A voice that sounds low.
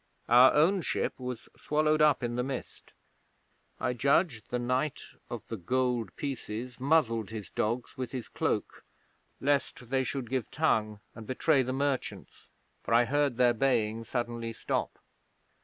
Yes: low, 125 Hz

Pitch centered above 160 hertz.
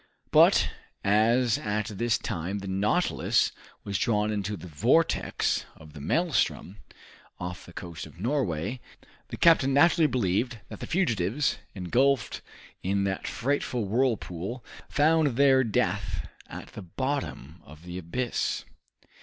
No: low, 105 Hz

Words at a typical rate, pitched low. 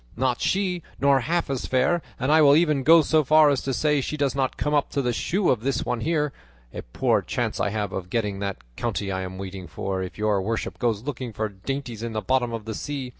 No: fast, 245 wpm; low, 130 Hz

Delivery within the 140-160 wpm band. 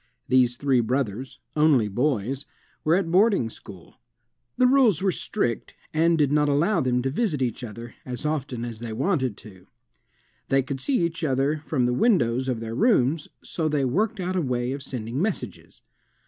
No: average, 175 wpm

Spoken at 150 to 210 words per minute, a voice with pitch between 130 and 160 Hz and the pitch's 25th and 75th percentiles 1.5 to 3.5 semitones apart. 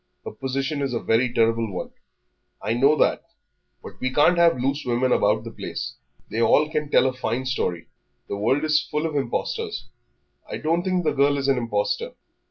No: average, 190 wpm; low, 135 Hz; average, 4.1 semitones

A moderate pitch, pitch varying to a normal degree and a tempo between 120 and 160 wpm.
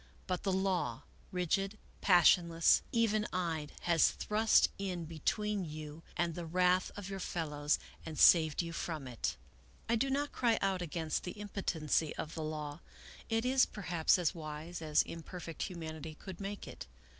Yes: medium, 175 Hz; average, 3.7 semitones; average, 155 wpm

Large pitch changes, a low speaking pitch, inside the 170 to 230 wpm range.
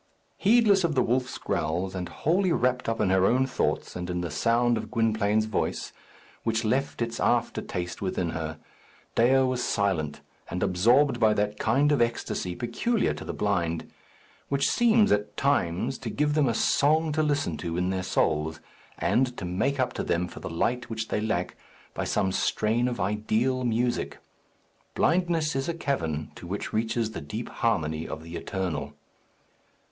Yes: wide, 6.6 semitones; low, 110 Hz; average, 175 wpm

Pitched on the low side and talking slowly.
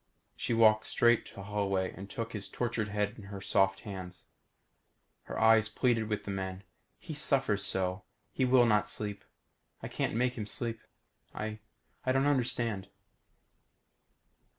No: low, 105 Hz; average, 150 wpm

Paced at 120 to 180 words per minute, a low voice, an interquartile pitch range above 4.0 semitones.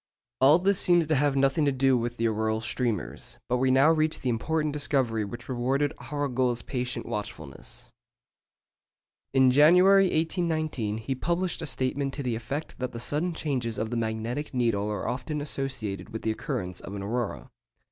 Yes: average, 170 wpm; low, 130 Hz; average, 4.5 semitones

